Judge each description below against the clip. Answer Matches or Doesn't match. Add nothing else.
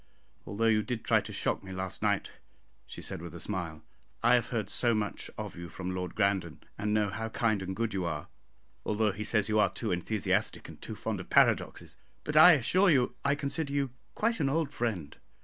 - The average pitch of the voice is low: Matches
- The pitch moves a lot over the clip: Doesn't match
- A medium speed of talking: Doesn't match